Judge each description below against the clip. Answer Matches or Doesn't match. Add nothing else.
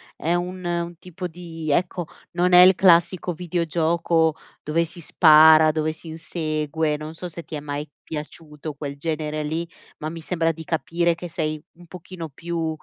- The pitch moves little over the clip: Matches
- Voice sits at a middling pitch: Matches